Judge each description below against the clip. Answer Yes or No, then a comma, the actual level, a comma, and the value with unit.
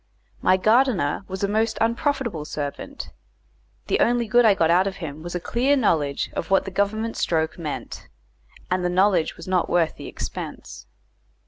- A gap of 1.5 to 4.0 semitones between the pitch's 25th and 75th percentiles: No, average, 5.1 semitones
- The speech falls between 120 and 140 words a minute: No, average, 170 wpm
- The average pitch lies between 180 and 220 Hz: Yes, high, 190 Hz